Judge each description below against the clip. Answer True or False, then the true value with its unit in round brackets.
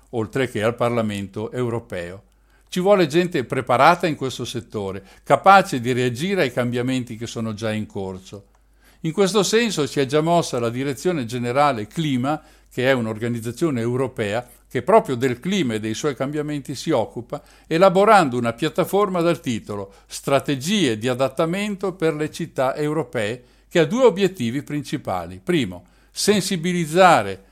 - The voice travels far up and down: True (6.2 semitones)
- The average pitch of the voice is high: False (135 Hz)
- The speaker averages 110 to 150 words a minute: True (145 wpm)